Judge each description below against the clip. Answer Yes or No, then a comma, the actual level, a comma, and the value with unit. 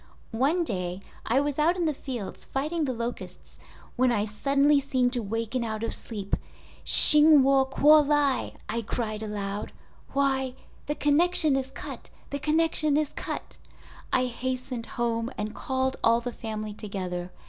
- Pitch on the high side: Yes, very high, 255 Hz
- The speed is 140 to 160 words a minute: Yes, average, 150 wpm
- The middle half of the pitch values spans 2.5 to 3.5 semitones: No, average, 4.3 semitones